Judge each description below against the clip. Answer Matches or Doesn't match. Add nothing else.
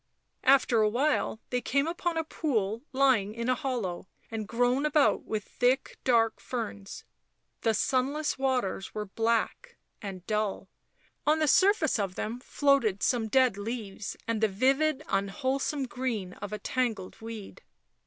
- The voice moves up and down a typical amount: Matches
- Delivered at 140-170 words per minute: Matches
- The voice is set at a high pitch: Matches